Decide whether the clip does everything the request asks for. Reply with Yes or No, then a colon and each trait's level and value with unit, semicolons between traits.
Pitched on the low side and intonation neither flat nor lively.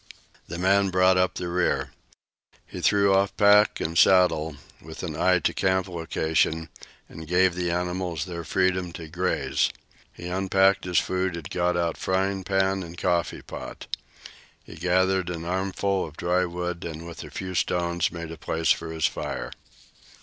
No: very low, 90 Hz; narrow, 1.7 semitones